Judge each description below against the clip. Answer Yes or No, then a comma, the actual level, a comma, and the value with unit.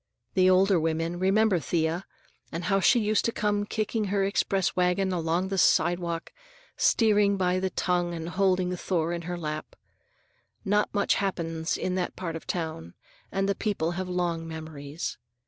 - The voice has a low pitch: No, medium, 180 Hz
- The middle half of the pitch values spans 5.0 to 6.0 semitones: No, average, 2.8 semitones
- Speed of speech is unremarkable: Yes, average, 165 wpm